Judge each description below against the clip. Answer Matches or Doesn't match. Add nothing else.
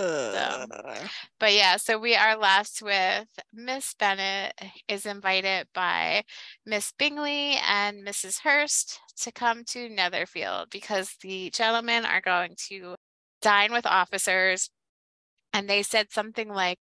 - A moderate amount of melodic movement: Matches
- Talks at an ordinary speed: Doesn't match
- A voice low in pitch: Doesn't match